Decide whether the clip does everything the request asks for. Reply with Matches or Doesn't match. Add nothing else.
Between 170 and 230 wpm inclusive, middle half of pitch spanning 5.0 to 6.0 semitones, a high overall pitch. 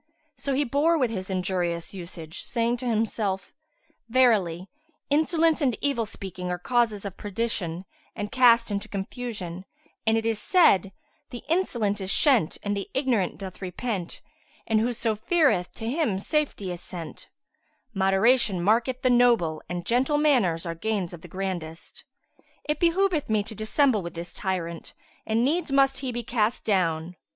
Doesn't match